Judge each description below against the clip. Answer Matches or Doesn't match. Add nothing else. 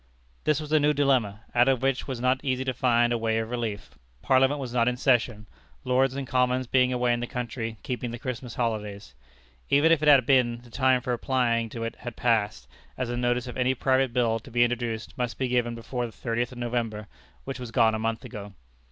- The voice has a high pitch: Doesn't match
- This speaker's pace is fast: Matches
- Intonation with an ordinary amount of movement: Doesn't match